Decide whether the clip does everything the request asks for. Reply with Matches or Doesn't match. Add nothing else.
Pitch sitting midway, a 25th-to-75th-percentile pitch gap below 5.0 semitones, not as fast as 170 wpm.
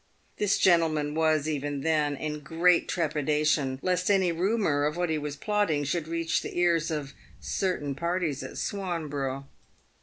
Matches